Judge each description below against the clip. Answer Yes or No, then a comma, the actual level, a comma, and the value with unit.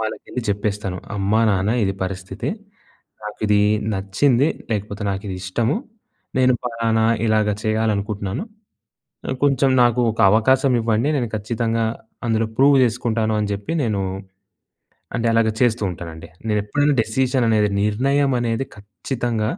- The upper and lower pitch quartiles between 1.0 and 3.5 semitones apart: Yes, average, 2.7 semitones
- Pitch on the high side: No, low, 110 Hz